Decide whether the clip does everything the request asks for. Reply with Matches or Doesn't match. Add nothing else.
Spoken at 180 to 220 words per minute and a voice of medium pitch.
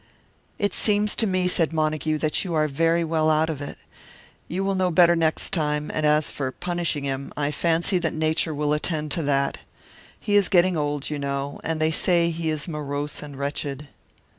Matches